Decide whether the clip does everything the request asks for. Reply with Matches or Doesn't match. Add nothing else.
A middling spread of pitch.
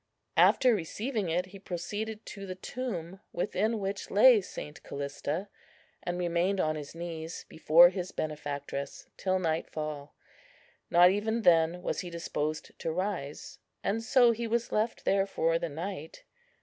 Matches